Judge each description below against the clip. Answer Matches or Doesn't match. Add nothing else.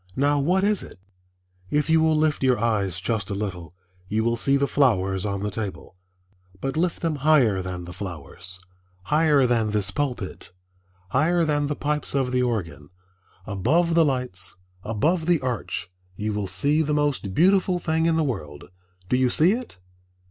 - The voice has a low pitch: Matches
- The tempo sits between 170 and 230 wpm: Matches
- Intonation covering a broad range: Matches